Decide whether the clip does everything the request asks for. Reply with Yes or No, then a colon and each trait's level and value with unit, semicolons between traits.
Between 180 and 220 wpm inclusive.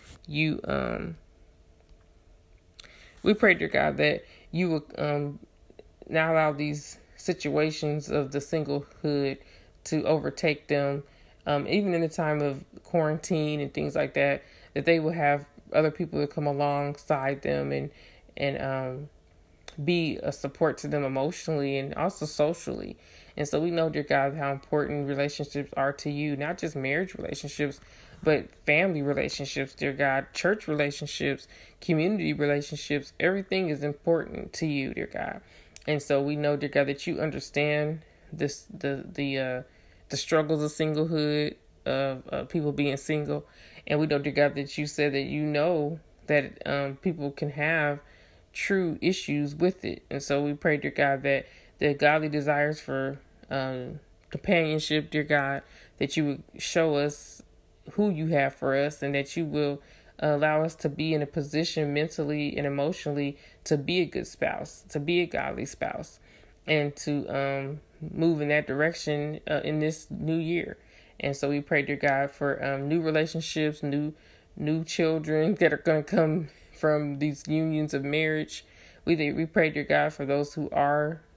No: average, 165 wpm